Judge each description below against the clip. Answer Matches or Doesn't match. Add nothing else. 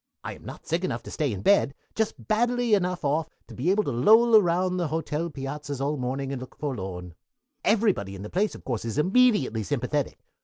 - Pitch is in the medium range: Matches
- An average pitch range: Doesn't match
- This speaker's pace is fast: Matches